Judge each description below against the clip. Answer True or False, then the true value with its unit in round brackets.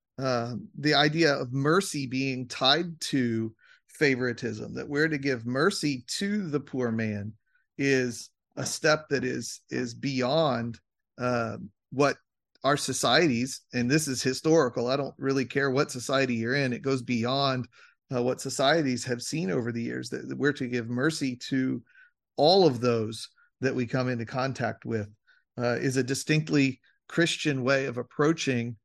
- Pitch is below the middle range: True (130 Hz)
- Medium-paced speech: True (155 wpm)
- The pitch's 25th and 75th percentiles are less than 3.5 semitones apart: True (2.9 semitones)